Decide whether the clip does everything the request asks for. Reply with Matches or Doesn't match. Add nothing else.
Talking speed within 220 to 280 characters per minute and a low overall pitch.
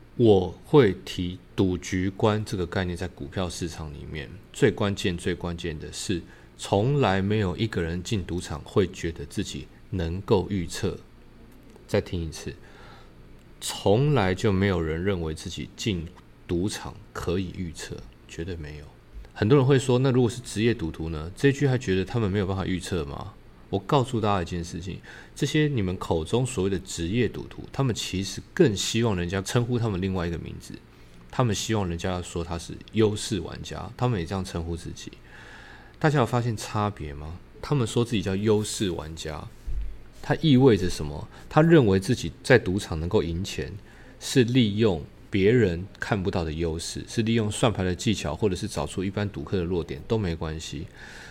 Matches